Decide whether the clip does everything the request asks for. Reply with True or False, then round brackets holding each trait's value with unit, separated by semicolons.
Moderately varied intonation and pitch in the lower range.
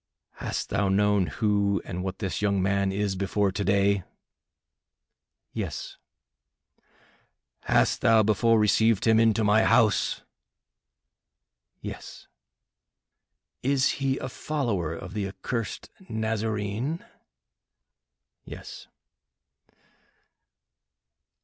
False (2.3 semitones; 105 Hz)